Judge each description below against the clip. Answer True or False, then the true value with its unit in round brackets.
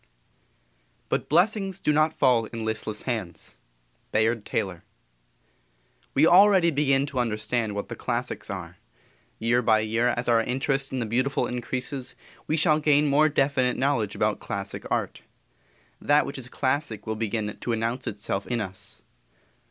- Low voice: True (125 Hz)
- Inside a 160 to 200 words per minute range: False (150 wpm)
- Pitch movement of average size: True (4.5 semitones)